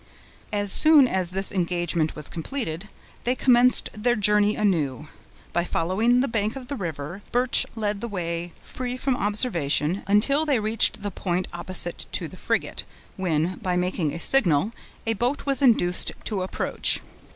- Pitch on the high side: Yes, high, 200 Hz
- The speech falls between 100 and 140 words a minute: No, average, 160 wpm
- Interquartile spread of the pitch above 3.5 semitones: Yes, wide, 5.6 semitones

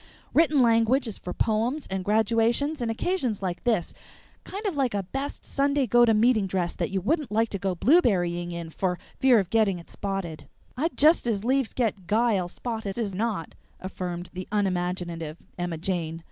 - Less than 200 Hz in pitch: No, high, 210 Hz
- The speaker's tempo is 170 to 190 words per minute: Yes, average, 180 wpm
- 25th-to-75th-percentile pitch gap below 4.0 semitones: No, average, 5.1 semitones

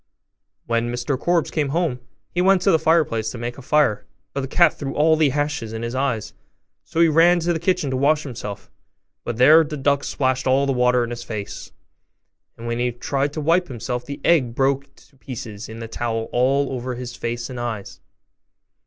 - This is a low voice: Yes, low, 130 Hz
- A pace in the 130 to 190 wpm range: No, fast, 205 wpm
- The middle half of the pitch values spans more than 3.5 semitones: Yes, average, 4.1 semitones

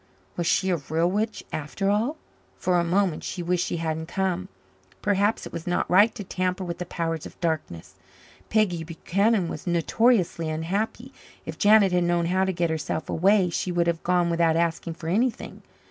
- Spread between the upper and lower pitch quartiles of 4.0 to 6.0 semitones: No, average, 2.9 semitones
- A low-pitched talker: No, medium, 175 Hz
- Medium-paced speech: Yes, average, 185 wpm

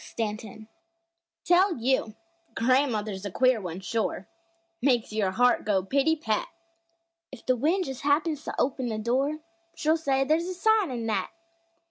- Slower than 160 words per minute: Yes, average, 150 wpm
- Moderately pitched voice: No, very high, 255 Hz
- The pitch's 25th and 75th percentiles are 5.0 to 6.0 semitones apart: Yes, wide, 5.5 semitones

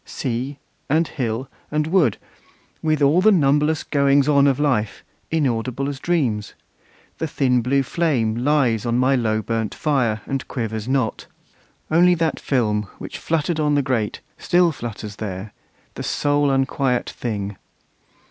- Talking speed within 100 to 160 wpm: Yes, average, 145 wpm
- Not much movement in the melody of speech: No, average, 4.7 semitones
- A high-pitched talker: No, low, 135 Hz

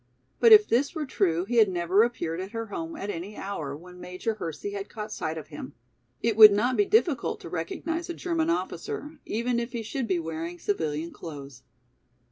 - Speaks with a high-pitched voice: Yes, high, 205 Hz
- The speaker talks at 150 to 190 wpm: No, average, 200 wpm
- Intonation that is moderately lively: No, wide, 7.0 semitones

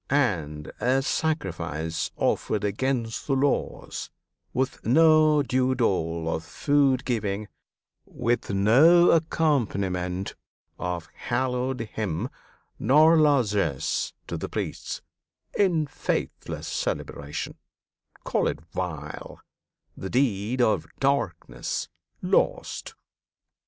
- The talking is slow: Yes, slow, 90 wpm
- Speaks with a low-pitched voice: Yes, low, 120 Hz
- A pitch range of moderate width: No, wide, 7.4 semitones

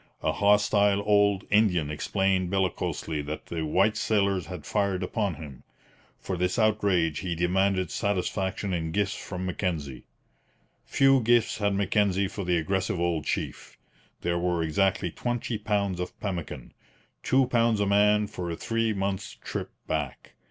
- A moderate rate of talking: Yes, average, 145 wpm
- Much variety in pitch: No, average, 2.9 semitones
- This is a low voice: Yes, very low, 95 Hz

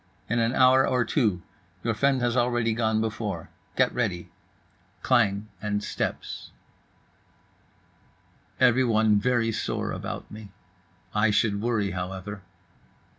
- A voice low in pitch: Yes, low, 110 Hz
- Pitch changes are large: No, average, 2.8 semitones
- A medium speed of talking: No, slow, 115 wpm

